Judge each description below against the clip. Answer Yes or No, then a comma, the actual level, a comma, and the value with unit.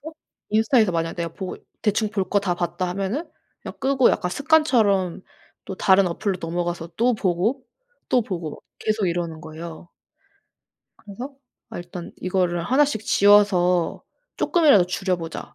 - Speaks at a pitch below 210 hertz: Yes, high, 190 Hz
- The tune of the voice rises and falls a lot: No, average, 4.1 semitones